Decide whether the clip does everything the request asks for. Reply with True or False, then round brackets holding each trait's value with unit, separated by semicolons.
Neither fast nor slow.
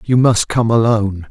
True (185 wpm)